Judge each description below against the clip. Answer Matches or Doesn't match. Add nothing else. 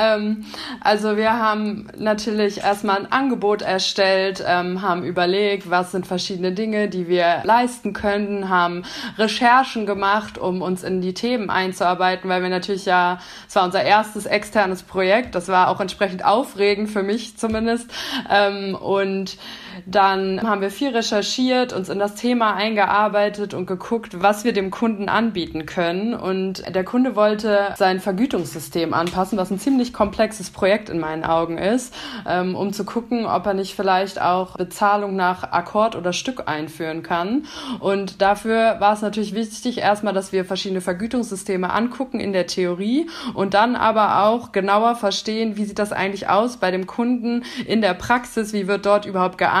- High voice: Matches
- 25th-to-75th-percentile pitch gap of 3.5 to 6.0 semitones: Doesn't match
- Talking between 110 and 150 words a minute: Doesn't match